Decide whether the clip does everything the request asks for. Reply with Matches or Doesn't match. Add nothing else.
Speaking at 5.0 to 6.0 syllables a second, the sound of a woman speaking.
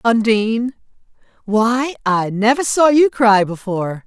Doesn't match